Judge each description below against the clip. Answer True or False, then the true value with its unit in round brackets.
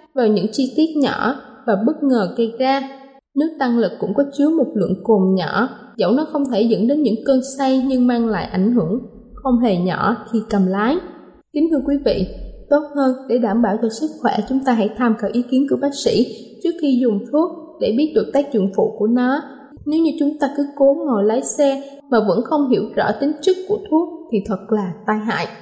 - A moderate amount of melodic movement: True (4.5 semitones)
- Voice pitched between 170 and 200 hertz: False (255 Hz)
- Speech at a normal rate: True (225 wpm)